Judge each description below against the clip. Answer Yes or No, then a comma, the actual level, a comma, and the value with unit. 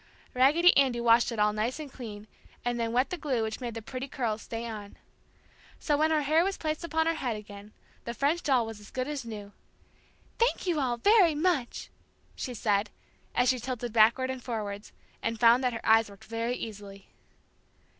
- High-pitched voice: Yes, high, 240 Hz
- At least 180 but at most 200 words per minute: Yes, average, 195 wpm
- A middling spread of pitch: Yes, average, 4.1 semitones